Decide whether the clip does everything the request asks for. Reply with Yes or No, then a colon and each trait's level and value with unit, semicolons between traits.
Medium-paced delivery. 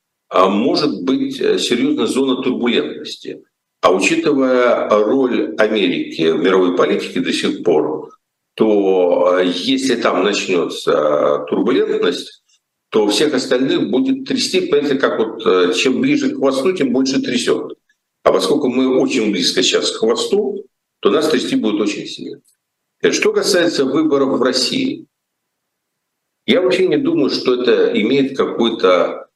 Yes: average, 125 wpm